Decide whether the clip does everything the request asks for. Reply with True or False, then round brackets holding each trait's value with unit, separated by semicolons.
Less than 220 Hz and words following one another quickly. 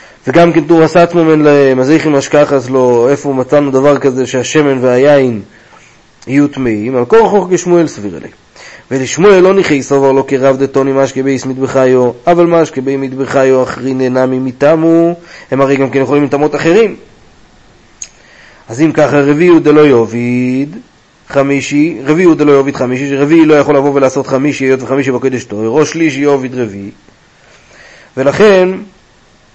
True (140 Hz; 155 wpm)